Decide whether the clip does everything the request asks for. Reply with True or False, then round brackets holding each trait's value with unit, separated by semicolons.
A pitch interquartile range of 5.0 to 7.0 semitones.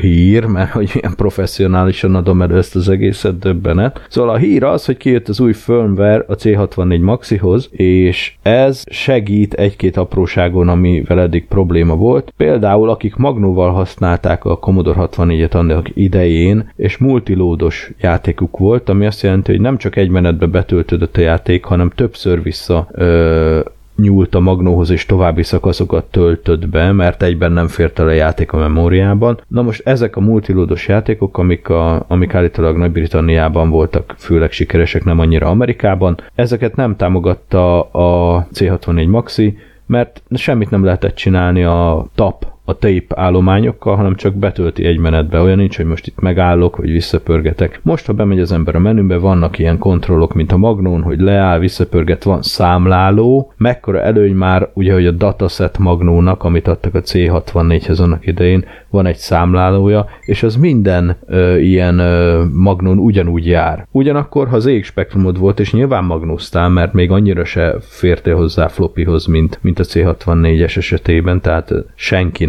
False (2.8 semitones)